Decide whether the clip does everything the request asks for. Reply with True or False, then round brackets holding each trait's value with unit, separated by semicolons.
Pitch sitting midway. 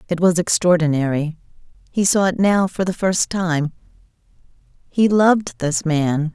True (170 Hz)